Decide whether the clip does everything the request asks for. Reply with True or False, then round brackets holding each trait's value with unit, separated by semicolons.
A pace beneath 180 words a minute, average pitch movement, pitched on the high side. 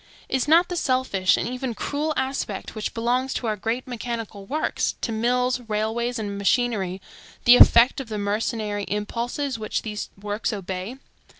True (160 wpm; 3.3 semitones; 230 Hz)